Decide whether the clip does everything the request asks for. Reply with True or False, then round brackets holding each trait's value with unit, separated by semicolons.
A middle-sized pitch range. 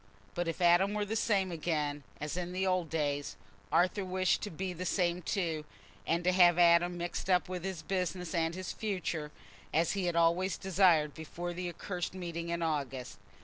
False (2.2 semitones)